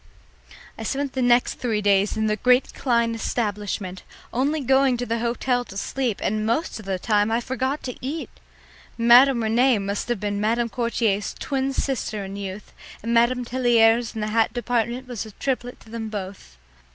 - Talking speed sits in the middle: Yes, average, 175 wpm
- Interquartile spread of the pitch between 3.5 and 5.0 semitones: No, average, 2.9 semitones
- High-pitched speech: Yes, high, 235 Hz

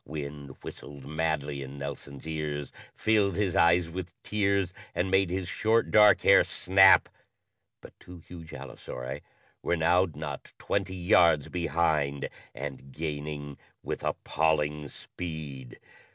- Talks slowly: Yes, slow, 125 wpm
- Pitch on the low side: Yes, very low, 80 Hz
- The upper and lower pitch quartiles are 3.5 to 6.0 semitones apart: Yes, average, 3.8 semitones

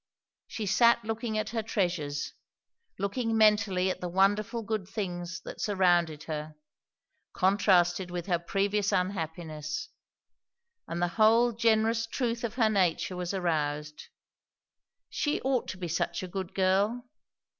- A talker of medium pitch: No, high, 195 Hz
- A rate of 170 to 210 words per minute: No, slow, 135 wpm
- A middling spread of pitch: Yes, average, 4.0 semitones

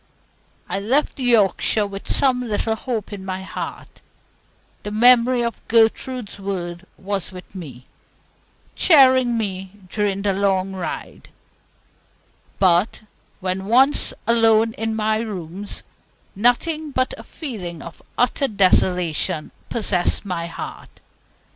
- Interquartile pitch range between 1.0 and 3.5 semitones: No, average, 3.9 semitones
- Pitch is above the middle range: Yes, high, 205 Hz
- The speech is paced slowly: Yes, slow, 115 wpm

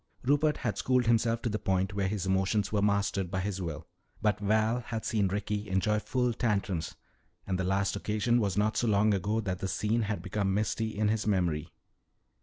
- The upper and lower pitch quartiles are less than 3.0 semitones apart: Yes, narrow, 2.4 semitones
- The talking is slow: No, average, 200 wpm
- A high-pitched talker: No, low, 105 Hz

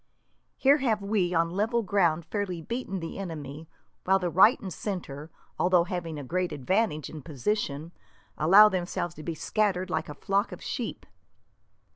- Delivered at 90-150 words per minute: No, average, 160 wpm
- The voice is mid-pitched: Yes, medium, 180 Hz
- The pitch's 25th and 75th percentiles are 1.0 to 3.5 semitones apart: No, average, 4.0 semitones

